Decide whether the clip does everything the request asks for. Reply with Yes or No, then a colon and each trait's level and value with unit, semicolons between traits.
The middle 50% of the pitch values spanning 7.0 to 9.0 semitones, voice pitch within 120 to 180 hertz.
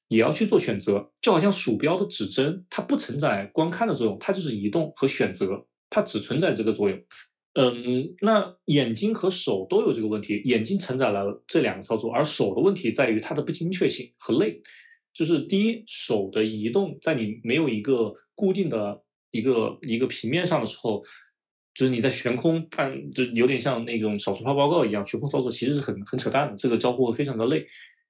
Yes: wide, 8.5 semitones; low, 135 Hz